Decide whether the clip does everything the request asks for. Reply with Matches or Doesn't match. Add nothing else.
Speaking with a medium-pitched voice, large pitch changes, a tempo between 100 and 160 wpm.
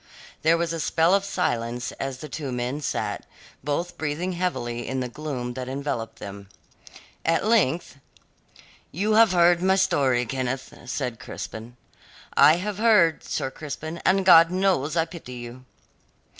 Matches